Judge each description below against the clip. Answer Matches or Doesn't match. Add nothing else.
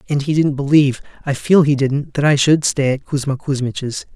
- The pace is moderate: Doesn't match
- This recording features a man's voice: Matches